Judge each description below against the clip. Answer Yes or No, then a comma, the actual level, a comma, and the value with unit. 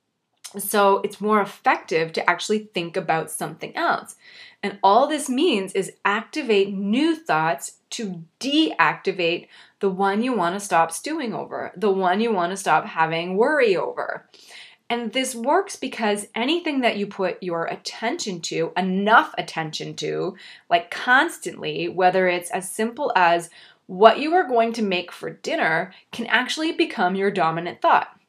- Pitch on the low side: No, high, 205 Hz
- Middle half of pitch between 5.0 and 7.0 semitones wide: Yes, average, 5.3 semitones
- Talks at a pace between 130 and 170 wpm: Yes, average, 155 wpm